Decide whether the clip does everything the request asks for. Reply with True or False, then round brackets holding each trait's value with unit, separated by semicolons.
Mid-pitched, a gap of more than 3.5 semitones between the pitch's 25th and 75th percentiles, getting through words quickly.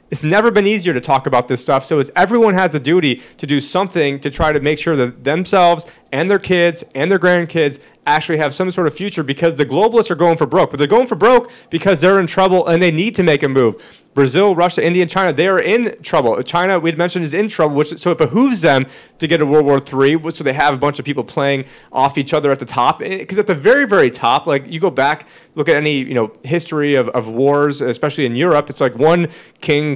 True (160 Hz; 4.0 semitones; 250 wpm)